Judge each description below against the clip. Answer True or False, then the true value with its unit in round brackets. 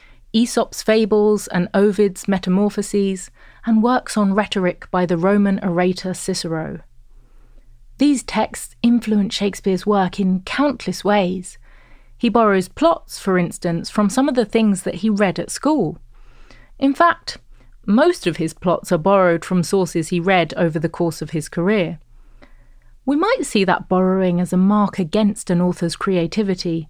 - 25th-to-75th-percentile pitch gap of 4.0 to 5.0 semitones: False (3.2 semitones)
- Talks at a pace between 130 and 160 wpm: True (150 wpm)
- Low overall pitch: False (195 Hz)